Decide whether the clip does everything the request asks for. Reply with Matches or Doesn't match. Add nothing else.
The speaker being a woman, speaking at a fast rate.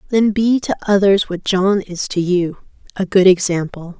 Doesn't match